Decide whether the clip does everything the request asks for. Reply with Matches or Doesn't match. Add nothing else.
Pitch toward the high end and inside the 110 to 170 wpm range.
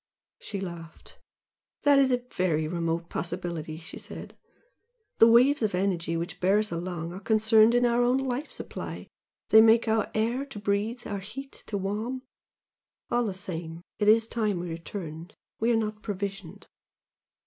Matches